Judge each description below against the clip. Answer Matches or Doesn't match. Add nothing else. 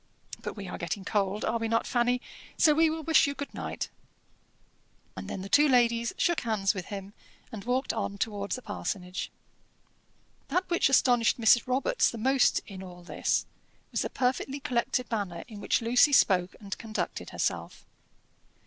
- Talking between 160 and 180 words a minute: Matches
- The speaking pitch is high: Matches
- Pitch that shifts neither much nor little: Matches